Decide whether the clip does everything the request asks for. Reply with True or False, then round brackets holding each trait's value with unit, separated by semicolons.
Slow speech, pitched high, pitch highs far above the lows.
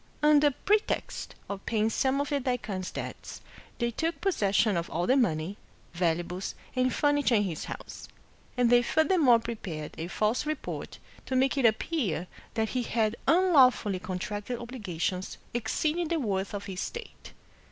False (150 wpm; 235 Hz; 6.4 semitones)